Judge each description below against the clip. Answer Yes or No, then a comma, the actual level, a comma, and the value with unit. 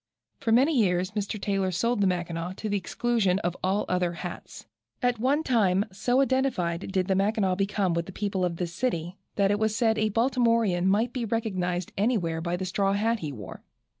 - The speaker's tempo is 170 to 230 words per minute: Yes, average, 200 wpm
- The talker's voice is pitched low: No, high, 195 Hz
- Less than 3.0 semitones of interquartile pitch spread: No, average, 4.1 semitones